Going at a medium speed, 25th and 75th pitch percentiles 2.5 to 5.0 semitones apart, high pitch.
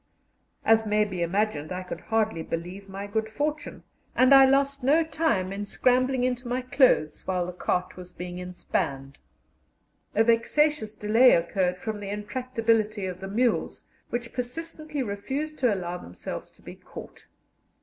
No: average, 155 wpm; wide, 5.6 semitones; high, 220 Hz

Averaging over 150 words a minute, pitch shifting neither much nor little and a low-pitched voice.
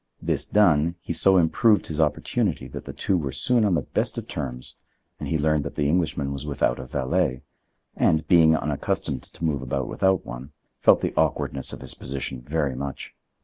Yes: average, 190 wpm; average, 3.6 semitones; very low, 75 Hz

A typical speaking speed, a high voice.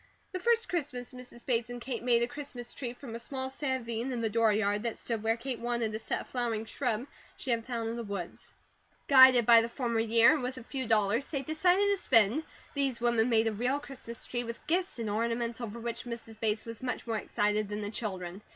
No: fast, 225 wpm; high, 235 Hz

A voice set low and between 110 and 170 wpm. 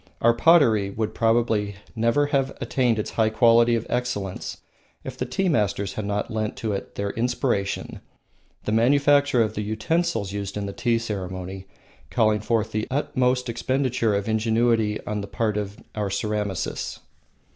Yes: low, 110 Hz; average, 155 wpm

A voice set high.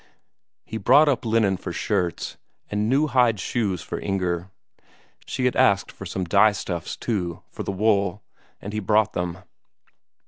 No: low, 100 Hz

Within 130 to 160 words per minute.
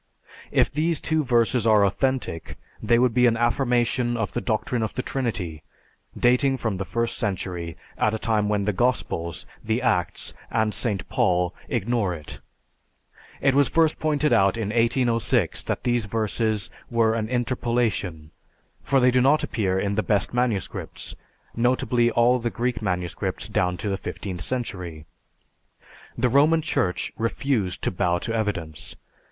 Yes: average, 155 wpm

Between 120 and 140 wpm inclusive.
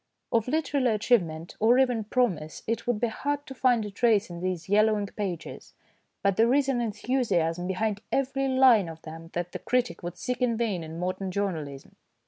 No: average, 190 wpm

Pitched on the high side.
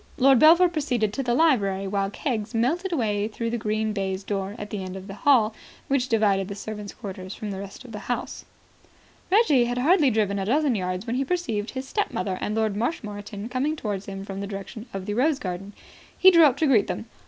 Yes: high, 215 Hz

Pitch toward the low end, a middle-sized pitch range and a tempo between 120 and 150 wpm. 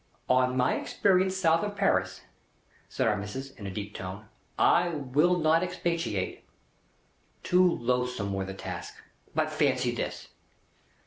No: low, 130 Hz; wide, 9.0 semitones; slow, 135 wpm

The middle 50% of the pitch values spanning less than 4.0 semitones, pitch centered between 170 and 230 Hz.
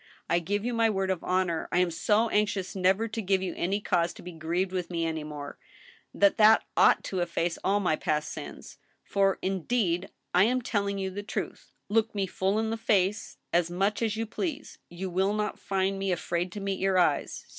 Yes: average, 2.9 semitones; high, 190 Hz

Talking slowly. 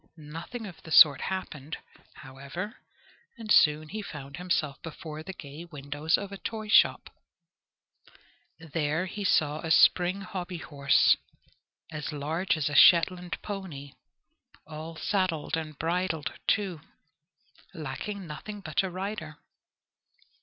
Yes: slow, 115 wpm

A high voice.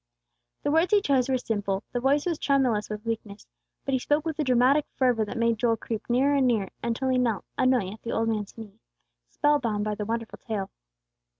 Yes: high, 240 Hz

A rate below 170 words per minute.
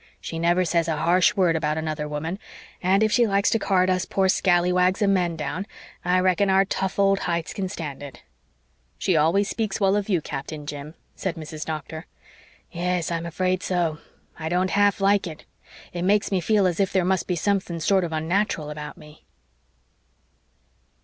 No: average, 185 wpm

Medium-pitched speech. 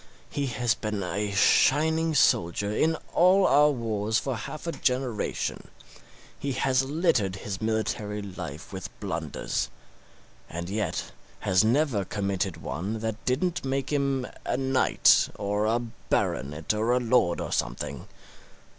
No: low, 110 Hz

